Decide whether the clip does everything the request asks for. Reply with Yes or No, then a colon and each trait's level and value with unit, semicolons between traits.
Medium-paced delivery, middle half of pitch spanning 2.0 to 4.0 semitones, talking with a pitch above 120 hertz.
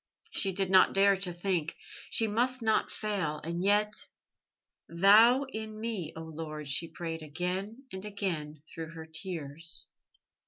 No: average, 145 wpm; average, 4.4 semitones; medium, 185 Hz